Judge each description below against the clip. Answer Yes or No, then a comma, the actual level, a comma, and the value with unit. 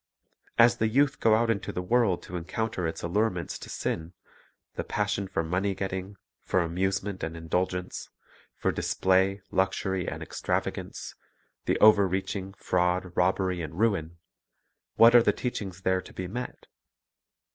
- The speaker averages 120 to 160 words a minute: Yes, average, 150 wpm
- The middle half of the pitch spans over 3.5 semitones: No, narrow, 2.5 semitones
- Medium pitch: No, very low, 95 Hz